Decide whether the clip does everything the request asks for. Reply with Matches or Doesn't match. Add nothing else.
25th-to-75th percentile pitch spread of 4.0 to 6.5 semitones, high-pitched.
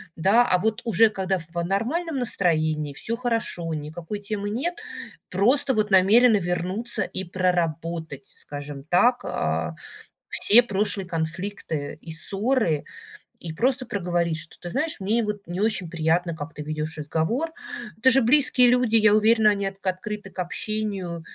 Matches